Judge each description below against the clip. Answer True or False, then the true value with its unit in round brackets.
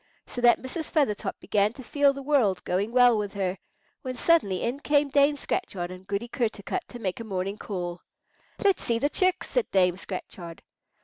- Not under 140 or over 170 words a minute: False (185 wpm)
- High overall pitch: True (230 Hz)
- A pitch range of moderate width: False (6.5 semitones)